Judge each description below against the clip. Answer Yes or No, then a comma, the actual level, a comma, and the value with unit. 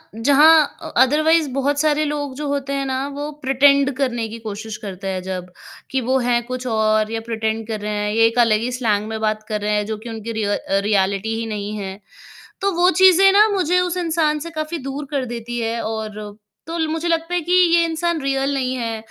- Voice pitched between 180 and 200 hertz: No, very high, 255 Hz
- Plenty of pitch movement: Yes, wide, 5.7 semitones